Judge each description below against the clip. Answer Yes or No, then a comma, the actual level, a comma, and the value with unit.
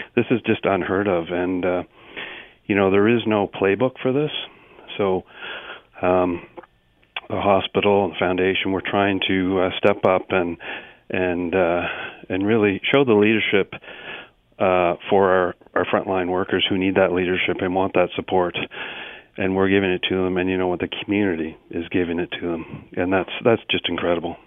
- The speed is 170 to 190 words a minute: Yes, average, 175 wpm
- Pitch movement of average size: No, narrow, 1.8 semitones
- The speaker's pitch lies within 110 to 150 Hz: No, very low, 95 Hz